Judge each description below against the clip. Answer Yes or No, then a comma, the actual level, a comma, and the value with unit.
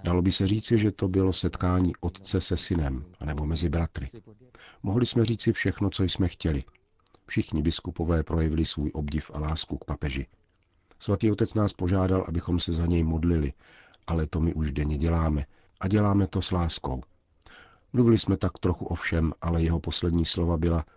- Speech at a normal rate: No, fast, 175 wpm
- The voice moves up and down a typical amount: Yes, average, 3.2 semitones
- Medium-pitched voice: No, very low, 85 Hz